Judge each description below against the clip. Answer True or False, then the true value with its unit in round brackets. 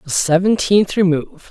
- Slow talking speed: True (120 wpm)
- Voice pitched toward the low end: False (180 Hz)